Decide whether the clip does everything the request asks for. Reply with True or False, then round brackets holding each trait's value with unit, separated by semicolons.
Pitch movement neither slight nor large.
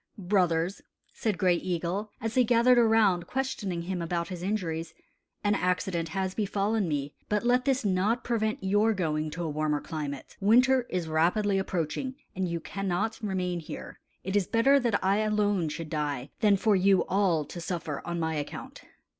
True (4.1 semitones)